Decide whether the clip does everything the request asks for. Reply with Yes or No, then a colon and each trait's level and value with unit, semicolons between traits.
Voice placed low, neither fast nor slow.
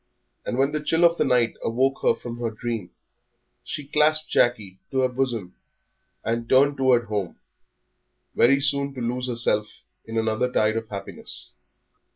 Yes: low, 120 Hz; average, 160 wpm